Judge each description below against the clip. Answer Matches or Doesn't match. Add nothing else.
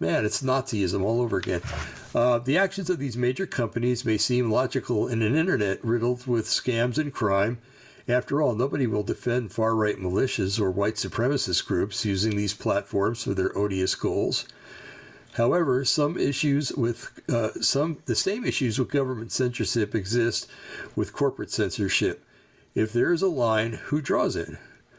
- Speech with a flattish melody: Doesn't match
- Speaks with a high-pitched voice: Doesn't match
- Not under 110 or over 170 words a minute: Matches